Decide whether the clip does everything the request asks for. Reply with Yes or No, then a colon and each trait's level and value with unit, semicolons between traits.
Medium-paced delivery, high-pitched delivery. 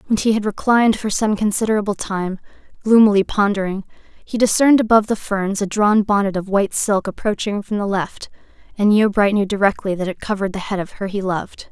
Yes: average, 195 wpm; high, 205 Hz